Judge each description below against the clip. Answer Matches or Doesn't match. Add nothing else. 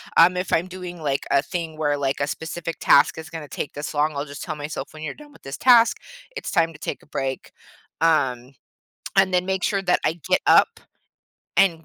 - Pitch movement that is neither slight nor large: Matches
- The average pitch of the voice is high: Doesn't match